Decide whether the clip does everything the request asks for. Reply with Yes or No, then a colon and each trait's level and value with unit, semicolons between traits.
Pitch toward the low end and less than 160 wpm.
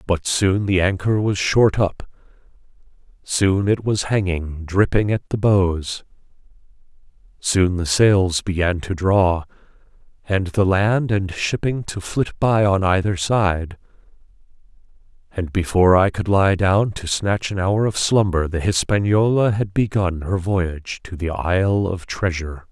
Yes: very low, 95 Hz; average, 145 wpm